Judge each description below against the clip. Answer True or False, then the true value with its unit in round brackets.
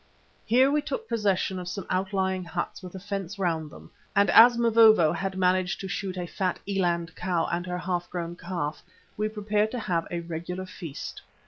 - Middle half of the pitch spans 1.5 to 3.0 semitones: True (2.7 semitones)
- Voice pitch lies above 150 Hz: True (185 Hz)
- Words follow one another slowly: False (190 wpm)